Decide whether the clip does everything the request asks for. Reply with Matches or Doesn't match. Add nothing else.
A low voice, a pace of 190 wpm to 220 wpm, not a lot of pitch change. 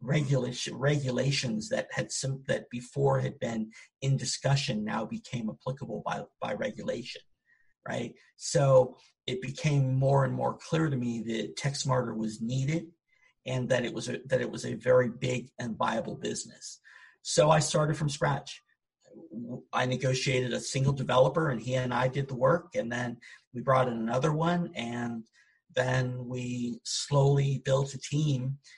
Doesn't match